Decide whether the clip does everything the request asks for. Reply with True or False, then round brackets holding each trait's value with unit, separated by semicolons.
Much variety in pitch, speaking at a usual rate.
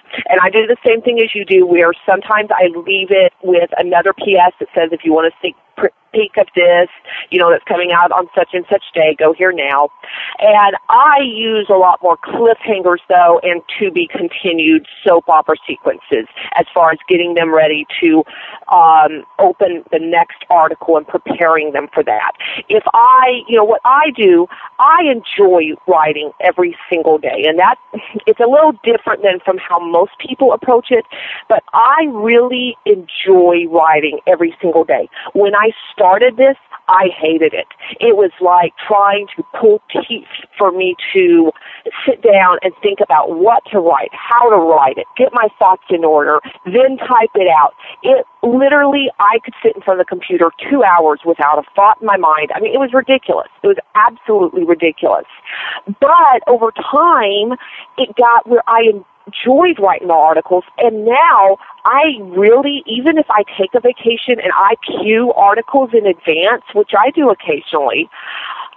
True (7.3 semitones; 175 wpm)